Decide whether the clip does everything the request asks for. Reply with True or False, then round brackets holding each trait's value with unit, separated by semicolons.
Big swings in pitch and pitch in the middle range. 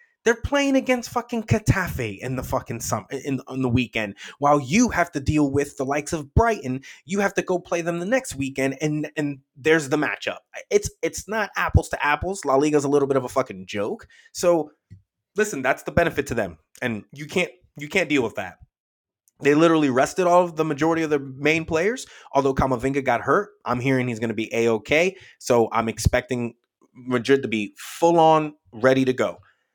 False (5.0 semitones; 145 Hz)